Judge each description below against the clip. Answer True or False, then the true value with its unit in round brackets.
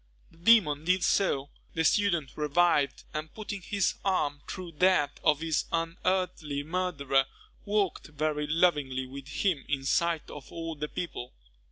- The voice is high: False (160 Hz)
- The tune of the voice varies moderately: True (4.0 semitones)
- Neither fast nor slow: True (145 wpm)